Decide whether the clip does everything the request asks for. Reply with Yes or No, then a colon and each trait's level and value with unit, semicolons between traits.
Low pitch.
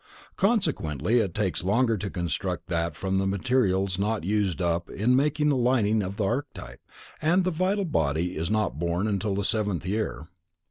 Yes: low, 100 Hz